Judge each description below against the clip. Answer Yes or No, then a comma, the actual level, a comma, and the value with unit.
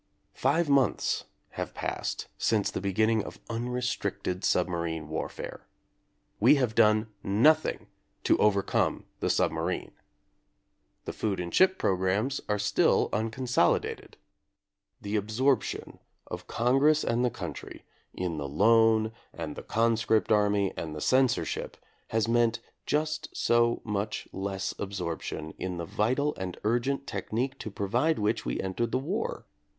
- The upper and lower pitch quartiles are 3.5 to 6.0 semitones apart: Yes, average, 4.3 semitones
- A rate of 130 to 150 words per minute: Yes, slow, 135 wpm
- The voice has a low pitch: Yes, low, 110 Hz